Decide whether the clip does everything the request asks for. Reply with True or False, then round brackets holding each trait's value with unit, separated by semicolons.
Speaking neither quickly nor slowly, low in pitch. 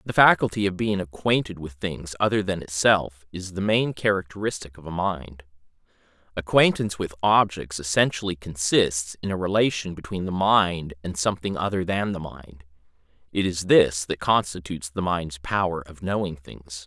True (160 wpm; 90 Hz)